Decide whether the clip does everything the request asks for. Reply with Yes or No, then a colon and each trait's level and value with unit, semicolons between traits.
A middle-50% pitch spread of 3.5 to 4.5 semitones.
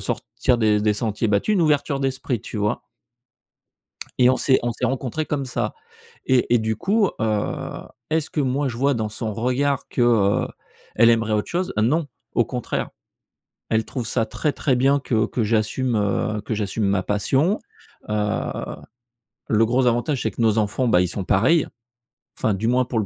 Yes: average, 3.8 semitones